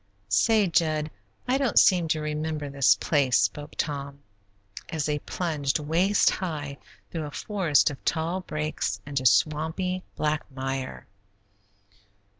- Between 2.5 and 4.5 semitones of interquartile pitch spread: Yes, average, 3.0 semitones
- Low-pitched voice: No, medium, 155 Hz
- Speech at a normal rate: No, slow, 125 wpm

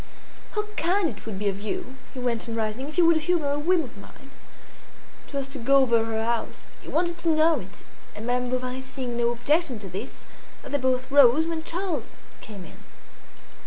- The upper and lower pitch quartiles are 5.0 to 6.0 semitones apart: Yes, wide, 5.6 semitones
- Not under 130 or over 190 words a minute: No, average, 200 wpm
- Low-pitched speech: No, very high, 260 Hz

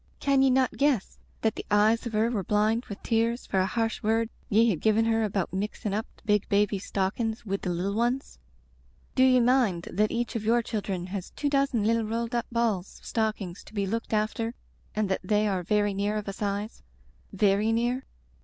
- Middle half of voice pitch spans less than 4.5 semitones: Yes, narrow, 2.5 semitones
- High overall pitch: Yes, high, 215 Hz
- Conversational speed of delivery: No, fast, 210 wpm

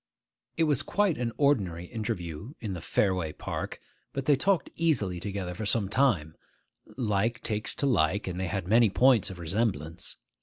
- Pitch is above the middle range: No, low, 105 Hz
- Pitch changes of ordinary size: No, wide, 6.2 semitones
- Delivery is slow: No, average, 165 wpm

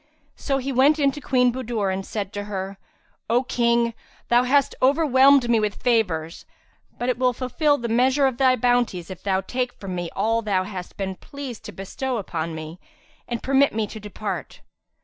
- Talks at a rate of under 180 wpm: No, average, 190 wpm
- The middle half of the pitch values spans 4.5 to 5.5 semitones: Yes, average, 4.8 semitones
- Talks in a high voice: Yes, high, 235 Hz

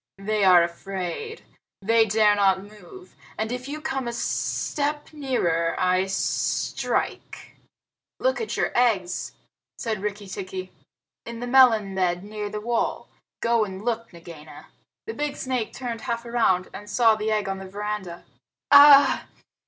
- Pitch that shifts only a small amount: No, average, 4.2 semitones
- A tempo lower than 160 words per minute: Yes, average, 150 wpm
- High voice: Yes, high, 215 Hz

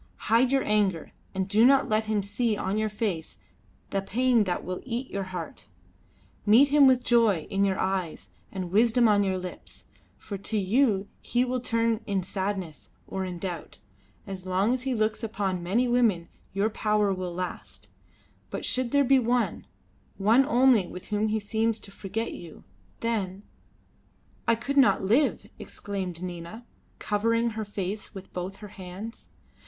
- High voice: Yes, high, 210 Hz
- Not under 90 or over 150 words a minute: No, average, 170 wpm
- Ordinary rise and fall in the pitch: Yes, average, 3.5 semitones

